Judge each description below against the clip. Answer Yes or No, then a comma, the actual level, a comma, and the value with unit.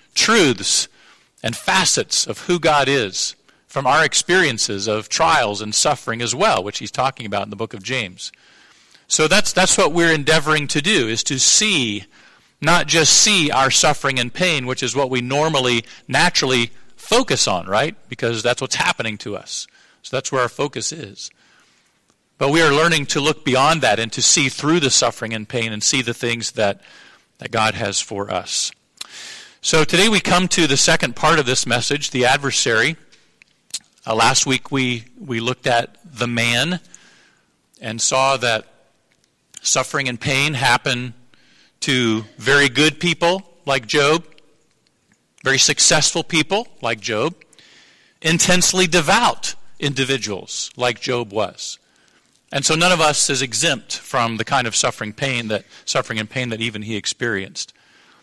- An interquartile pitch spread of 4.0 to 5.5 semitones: Yes, average, 4.9 semitones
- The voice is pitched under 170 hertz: Yes, low, 135 Hz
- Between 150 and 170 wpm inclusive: Yes, average, 160 wpm